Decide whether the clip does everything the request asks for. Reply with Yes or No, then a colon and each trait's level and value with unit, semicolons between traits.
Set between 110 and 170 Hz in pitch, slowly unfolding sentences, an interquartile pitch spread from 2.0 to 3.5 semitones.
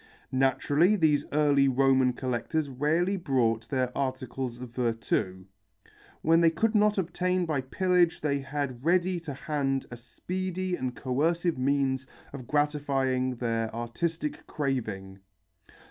No: medium, 140 Hz; slow, 125 wpm; average, 4.5 semitones